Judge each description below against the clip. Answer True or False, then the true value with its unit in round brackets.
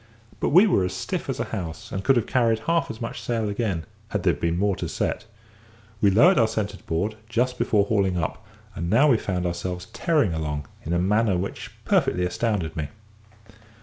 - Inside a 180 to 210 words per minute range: True (200 wpm)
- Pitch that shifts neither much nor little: True (4.6 semitones)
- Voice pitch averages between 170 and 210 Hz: False (100 Hz)